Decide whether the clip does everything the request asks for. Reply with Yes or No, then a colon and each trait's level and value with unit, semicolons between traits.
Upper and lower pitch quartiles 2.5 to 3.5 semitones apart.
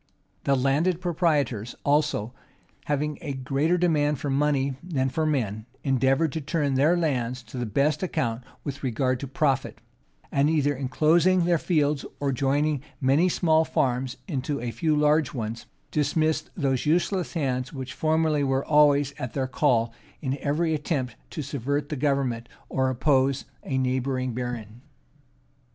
Yes: average, 2.9 semitones